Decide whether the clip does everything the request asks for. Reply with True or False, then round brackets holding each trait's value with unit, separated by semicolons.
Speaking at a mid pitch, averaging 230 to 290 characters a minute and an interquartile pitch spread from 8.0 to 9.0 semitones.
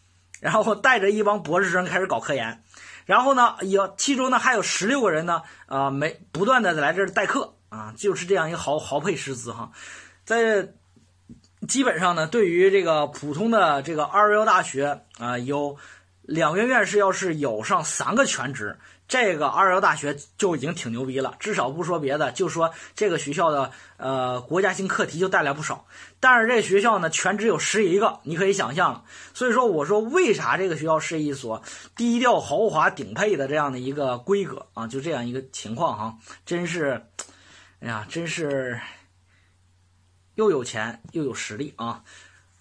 True (155 Hz; 270 characters per minute; 8.6 semitones)